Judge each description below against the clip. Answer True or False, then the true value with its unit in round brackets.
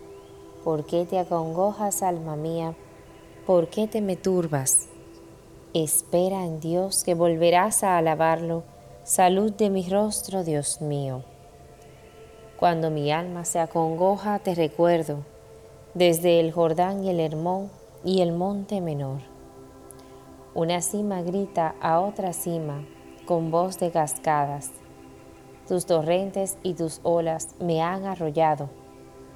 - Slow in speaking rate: True (120 wpm)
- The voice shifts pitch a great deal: False (3.9 semitones)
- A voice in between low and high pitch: True (165 Hz)